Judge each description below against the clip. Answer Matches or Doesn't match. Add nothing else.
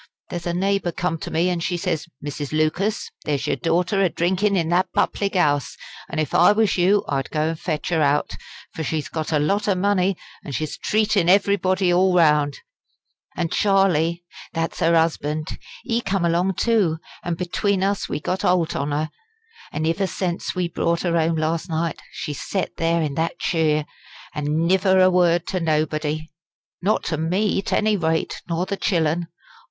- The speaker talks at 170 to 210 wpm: Matches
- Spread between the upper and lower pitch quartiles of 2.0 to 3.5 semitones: Matches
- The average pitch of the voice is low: Doesn't match